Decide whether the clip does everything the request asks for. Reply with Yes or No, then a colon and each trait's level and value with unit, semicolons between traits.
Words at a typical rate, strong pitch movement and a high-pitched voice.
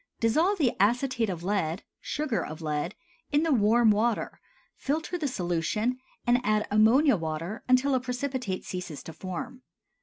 Yes: average, 150 wpm; wide, 5.9 semitones; high, 230 Hz